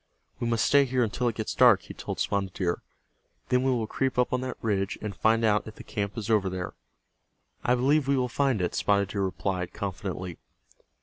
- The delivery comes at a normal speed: No, fast, 210 wpm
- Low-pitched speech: Yes, low, 110 Hz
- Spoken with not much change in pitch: No, average, 4.2 semitones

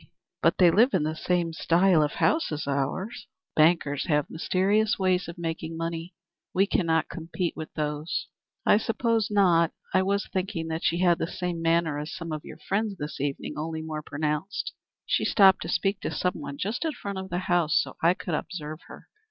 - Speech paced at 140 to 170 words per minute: No, average, 195 wpm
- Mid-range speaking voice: Yes, medium, 170 Hz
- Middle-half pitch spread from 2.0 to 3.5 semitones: Yes, average, 3.2 semitones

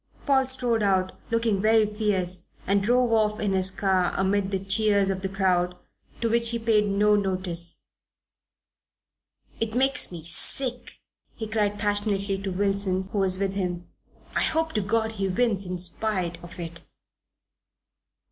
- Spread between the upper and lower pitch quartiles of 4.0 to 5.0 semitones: No, average, 2.8 semitones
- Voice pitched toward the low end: No, high, 200 Hz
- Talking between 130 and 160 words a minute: Yes, average, 155 wpm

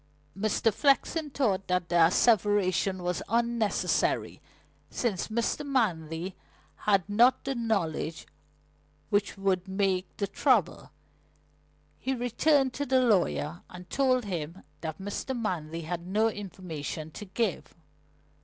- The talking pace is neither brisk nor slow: No, slow, 115 wpm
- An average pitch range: Yes, average, 4.9 semitones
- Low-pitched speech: No, high, 200 Hz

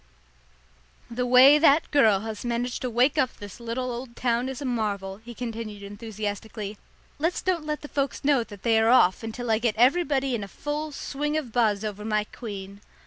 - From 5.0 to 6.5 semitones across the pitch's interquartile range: No, average, 3.9 semitones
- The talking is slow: No, average, 195 wpm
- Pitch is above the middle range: Yes, high, 235 Hz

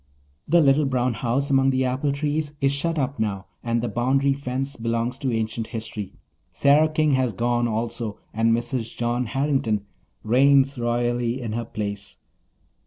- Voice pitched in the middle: No, low, 125 Hz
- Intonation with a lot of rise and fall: No, average, 3.1 semitones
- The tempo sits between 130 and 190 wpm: Yes, average, 160 wpm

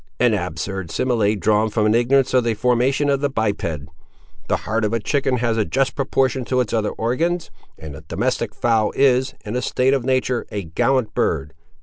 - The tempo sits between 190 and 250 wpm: Yes, average, 200 wpm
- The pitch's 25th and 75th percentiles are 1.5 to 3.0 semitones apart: No, average, 3.6 semitones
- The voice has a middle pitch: No, low, 120 Hz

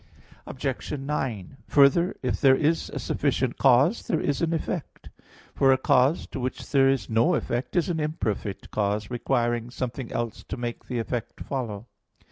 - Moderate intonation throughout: Yes, average, 3.3 semitones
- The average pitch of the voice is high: No, low, 130 Hz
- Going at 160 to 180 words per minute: Yes, average, 165 wpm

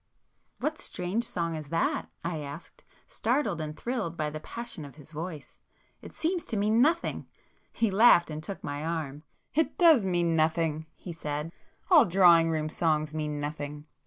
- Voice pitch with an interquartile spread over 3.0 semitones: Yes, average, 5.3 semitones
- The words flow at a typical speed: Yes, average, 160 wpm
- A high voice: No, medium, 165 Hz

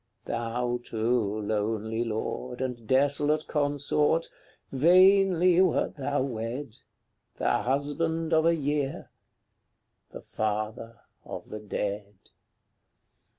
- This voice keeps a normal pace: No, slow, 95 wpm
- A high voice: No, low, 130 Hz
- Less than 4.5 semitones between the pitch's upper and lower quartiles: No, average, 5.2 semitones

